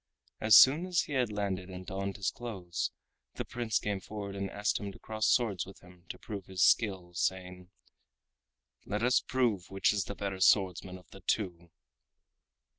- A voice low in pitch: Yes, low, 100 Hz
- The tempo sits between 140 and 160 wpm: No, average, 185 wpm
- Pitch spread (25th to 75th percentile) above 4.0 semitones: No, average, 2.8 semitones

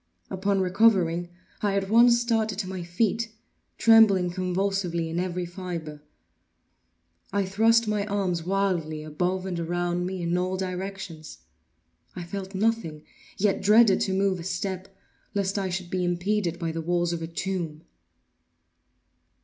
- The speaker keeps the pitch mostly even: Yes, narrow, 2.3 semitones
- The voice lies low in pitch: No, medium, 185 Hz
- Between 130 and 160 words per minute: Yes, average, 140 wpm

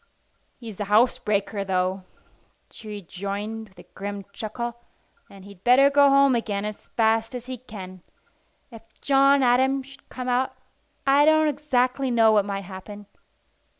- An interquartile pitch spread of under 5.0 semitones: Yes, average, 4.3 semitones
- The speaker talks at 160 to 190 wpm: No, average, 150 wpm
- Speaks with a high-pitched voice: Yes, high, 225 Hz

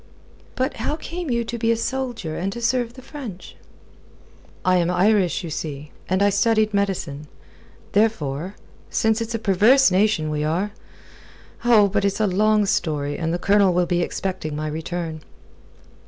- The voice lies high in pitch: Yes, high, 200 Hz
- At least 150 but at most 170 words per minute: Yes, average, 165 wpm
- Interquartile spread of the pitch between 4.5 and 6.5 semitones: Yes, average, 4.8 semitones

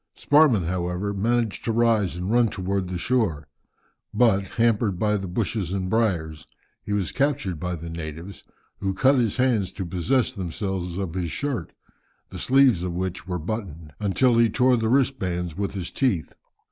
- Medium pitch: No, low, 100 Hz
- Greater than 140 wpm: Yes, average, 170 wpm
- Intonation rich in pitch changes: No, average, 4.7 semitones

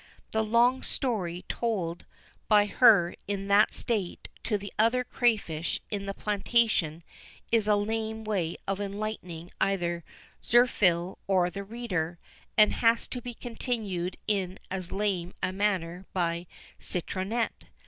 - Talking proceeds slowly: Yes, slow, 130 wpm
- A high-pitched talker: Yes, high, 200 Hz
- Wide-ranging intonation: No, average, 3.7 semitones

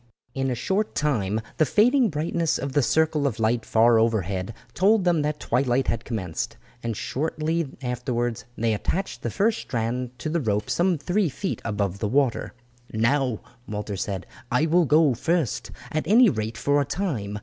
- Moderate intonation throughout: No, wide, 6.3 semitones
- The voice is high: No, low, 130 Hz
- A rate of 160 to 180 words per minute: Yes, average, 170 wpm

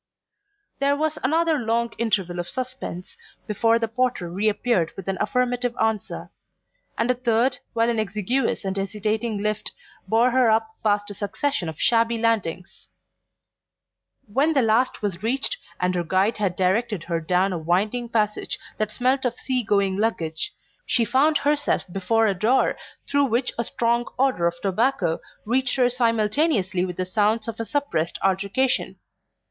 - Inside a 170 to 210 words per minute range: No, average, 155 wpm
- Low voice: No, high, 225 Hz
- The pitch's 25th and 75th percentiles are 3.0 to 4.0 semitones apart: No, average, 4.4 semitones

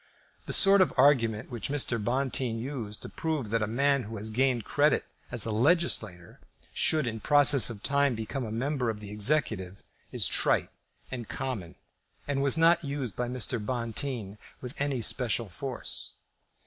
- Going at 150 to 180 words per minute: Yes, average, 165 wpm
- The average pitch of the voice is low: Yes, low, 125 Hz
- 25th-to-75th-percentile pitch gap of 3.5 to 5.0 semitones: Yes, average, 4.3 semitones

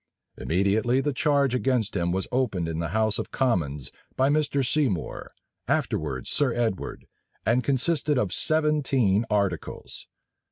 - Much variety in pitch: Yes, wide, 6.2 semitones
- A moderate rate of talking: No, slow, 130 wpm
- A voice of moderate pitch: No, low, 120 Hz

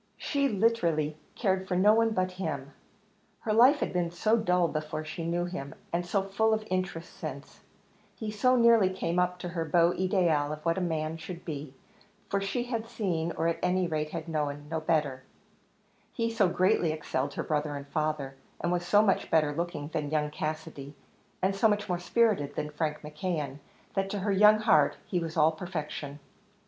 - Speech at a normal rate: Yes, average, 190 wpm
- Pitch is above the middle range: No, medium, 170 Hz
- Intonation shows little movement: No, average, 4.1 semitones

